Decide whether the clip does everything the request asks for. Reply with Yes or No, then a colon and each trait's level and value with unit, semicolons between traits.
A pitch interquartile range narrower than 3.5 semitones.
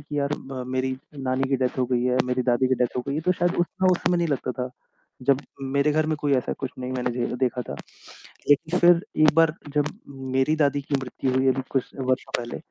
Yes: average, 2.9 semitones